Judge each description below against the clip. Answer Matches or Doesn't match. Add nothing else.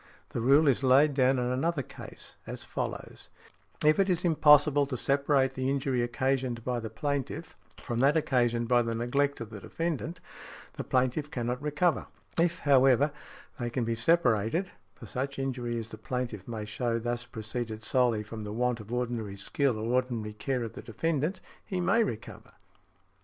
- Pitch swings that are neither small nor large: Matches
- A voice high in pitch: Doesn't match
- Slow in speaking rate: Doesn't match